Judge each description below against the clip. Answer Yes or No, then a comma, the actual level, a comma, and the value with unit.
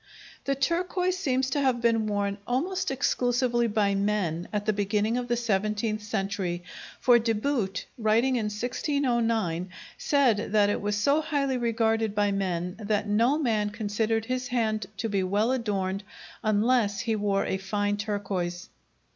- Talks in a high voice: Yes, high, 215 Hz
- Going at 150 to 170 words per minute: Yes, average, 155 wpm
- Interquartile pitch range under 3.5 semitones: Yes, average, 3.1 semitones